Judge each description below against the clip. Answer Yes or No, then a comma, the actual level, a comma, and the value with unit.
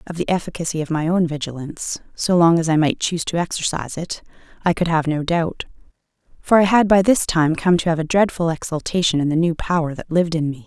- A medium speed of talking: No, fast, 230 wpm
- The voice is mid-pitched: Yes, medium, 165 Hz